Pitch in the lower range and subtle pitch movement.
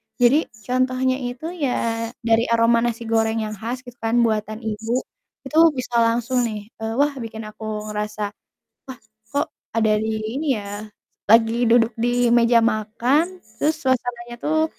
No: high, 235 Hz; narrow, 2.3 semitones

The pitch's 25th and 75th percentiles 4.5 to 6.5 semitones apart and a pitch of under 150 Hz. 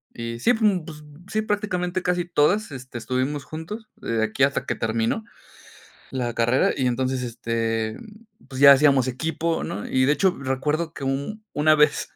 Yes: average, 5.2 semitones; medium, 140 Hz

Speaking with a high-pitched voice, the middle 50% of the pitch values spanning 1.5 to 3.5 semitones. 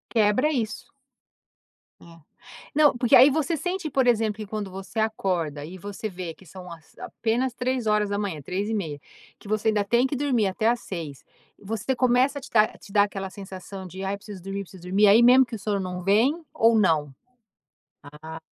No: high, 210 Hz; average, 4.2 semitones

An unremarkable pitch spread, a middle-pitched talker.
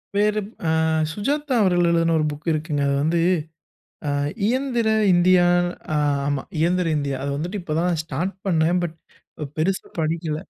Yes: average, 3.8 semitones; medium, 170 Hz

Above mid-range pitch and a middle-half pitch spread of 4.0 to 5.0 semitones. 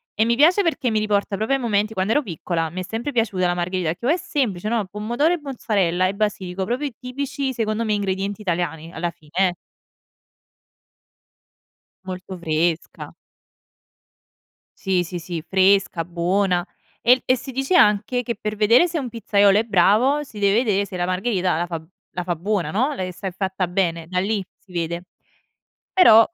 Yes: high, 200 Hz; average, 4.5 semitones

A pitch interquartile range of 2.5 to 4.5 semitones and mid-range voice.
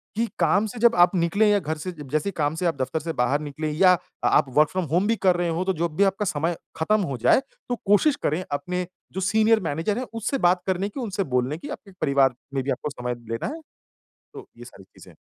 No: average, 5.2 semitones; medium, 175 Hz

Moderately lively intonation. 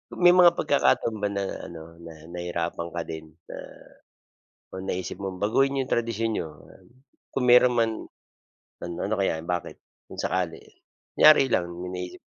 No: wide, 5.8 semitones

